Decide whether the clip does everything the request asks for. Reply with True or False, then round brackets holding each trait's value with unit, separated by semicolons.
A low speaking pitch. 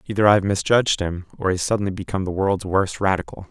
True (95 Hz)